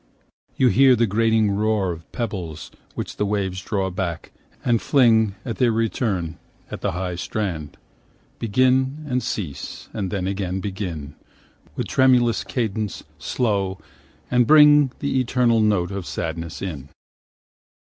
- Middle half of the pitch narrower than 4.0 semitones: No, average, 4.7 semitones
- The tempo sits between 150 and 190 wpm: No, slow, 135 wpm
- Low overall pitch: Yes, low, 105 Hz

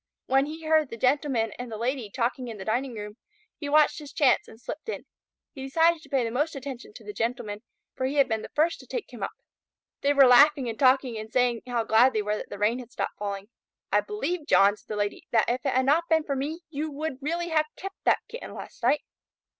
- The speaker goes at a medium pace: No, fast, 245 wpm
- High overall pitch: Yes, very high, 265 Hz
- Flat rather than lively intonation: No, average, 4.7 semitones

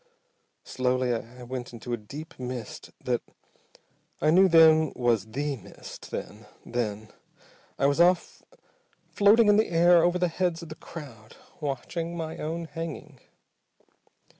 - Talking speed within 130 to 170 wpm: Yes, average, 140 wpm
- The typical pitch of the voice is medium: Yes, medium, 150 Hz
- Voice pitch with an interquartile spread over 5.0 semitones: Yes, wide, 5.6 semitones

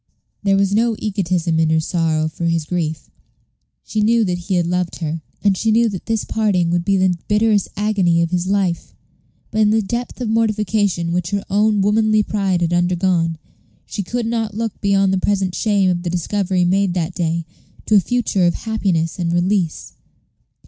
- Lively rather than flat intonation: No, average, 3.5 semitones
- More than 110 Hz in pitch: Yes, high, 190 Hz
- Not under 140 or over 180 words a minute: No, average, 190 wpm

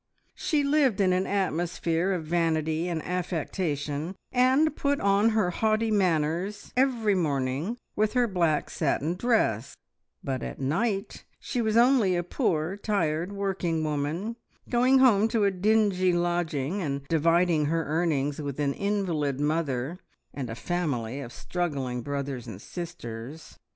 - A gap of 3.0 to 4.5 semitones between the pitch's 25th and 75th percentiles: No, wide, 5.5 semitones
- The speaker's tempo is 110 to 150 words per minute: Yes, average, 140 wpm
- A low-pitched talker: No, medium, 175 Hz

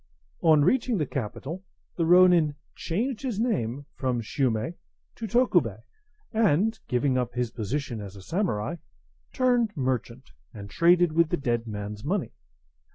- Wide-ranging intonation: Yes, wide, 7.9 semitones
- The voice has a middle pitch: Yes, medium, 145 Hz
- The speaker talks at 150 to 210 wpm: No, average, 140 wpm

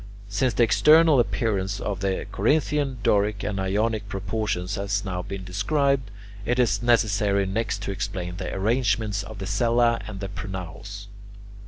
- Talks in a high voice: No, low, 105 Hz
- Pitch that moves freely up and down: No, average, 3.0 semitones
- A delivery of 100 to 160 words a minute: Yes, average, 150 wpm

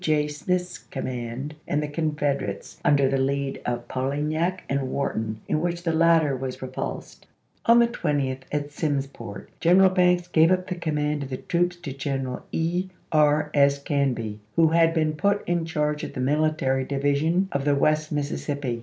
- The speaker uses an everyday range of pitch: Yes, average, 3.2 semitones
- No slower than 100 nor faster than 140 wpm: No, average, 180 wpm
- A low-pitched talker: No, medium, 150 Hz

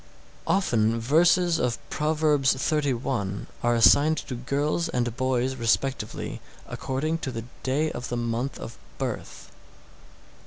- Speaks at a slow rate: Yes, slow, 130 wpm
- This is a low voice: Yes, low, 130 Hz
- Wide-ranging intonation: No, average, 4.2 semitones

